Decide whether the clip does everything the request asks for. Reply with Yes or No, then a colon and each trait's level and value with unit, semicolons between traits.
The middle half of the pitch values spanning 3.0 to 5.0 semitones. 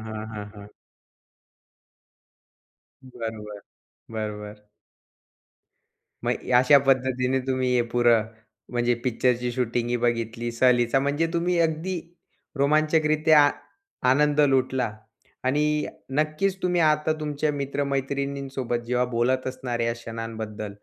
Yes: average, 3.7 semitones